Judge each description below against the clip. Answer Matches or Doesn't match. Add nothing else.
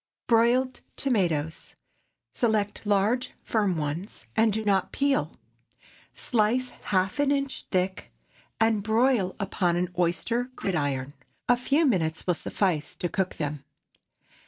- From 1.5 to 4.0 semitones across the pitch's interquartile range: Doesn't match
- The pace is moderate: Doesn't match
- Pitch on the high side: Matches